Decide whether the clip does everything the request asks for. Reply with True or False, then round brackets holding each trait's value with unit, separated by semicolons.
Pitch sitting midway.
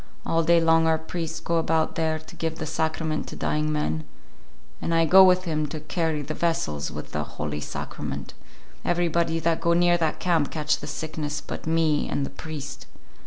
True (160 Hz)